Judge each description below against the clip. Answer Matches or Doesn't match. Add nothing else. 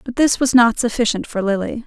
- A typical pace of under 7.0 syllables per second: Matches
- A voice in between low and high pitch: Doesn't match